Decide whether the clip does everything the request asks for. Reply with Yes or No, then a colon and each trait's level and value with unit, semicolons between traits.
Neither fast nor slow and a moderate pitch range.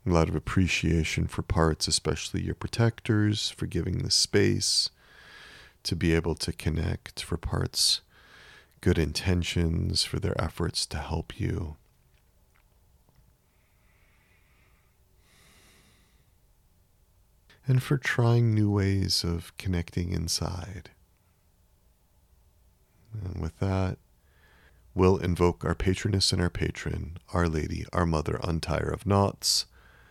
No: slow, 105 wpm; average, 3.1 semitones